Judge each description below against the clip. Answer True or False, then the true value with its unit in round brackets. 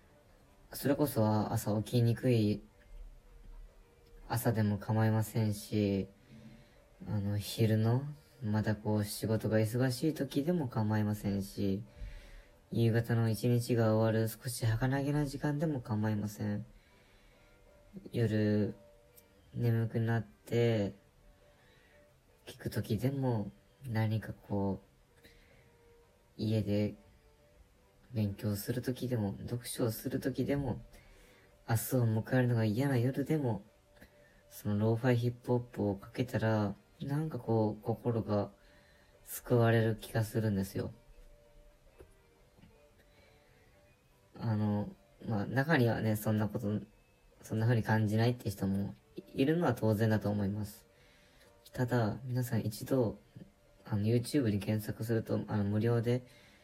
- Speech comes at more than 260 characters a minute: False (225 characters per minute)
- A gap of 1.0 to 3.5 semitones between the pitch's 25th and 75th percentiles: True (2.9 semitones)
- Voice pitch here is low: True (110 Hz)